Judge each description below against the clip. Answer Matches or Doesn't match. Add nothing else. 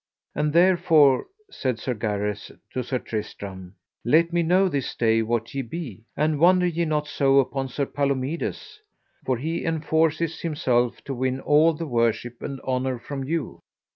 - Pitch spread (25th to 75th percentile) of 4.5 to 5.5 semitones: Matches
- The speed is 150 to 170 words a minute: Matches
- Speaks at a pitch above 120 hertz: Matches